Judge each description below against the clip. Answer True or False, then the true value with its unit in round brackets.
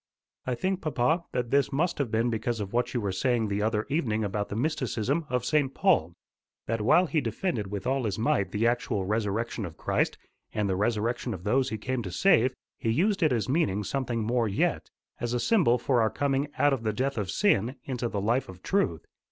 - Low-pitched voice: True (120 Hz)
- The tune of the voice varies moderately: True (4.3 semitones)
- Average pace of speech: False (215 wpm)